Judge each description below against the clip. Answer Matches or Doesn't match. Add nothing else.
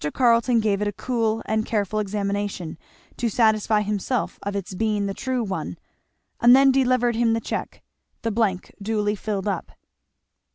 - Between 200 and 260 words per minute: Doesn't match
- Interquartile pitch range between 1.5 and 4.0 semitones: Matches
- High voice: Matches